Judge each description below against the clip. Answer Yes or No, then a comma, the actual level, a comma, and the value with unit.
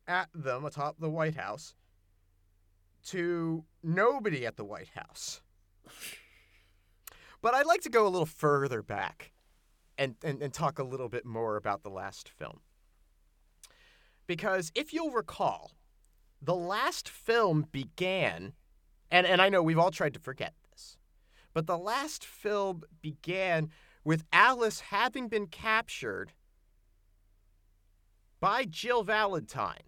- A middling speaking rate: No, slow, 130 wpm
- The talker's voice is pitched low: No, medium, 145 Hz